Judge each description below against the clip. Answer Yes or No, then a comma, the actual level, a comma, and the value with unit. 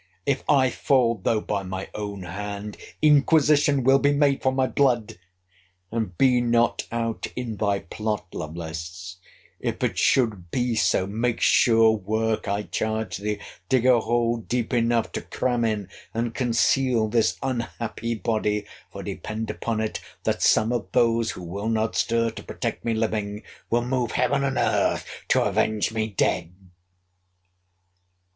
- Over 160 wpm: No, average, 150 wpm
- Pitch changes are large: No, narrow, 2.6 semitones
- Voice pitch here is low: Yes, low, 115 Hz